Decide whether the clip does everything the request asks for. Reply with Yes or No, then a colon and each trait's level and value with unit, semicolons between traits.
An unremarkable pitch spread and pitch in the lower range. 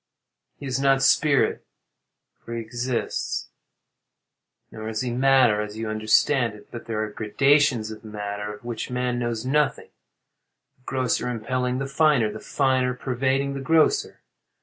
Yes: average, 3.6 semitones; low, 125 Hz